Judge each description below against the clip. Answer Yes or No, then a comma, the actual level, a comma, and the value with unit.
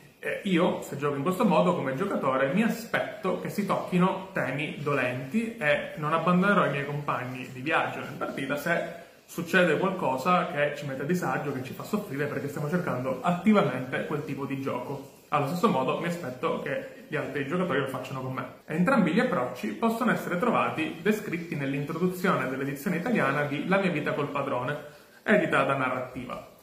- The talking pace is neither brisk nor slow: No, fast, 180 wpm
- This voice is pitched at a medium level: Yes, medium, 150 Hz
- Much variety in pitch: No, average, 4.8 semitones